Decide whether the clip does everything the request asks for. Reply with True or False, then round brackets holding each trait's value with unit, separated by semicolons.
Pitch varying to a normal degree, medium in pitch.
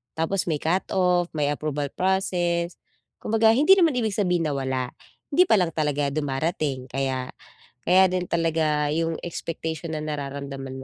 True (4.0 semitones; 160 Hz)